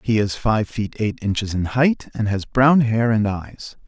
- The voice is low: Yes, low, 110 Hz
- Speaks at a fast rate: Yes, fast, 215 wpm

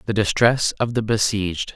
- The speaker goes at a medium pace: Yes, average, 170 wpm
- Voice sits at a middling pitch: No, low, 110 Hz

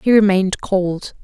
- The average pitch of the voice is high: Yes, high, 195 Hz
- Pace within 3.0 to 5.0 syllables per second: Yes, 4.6 syllables/s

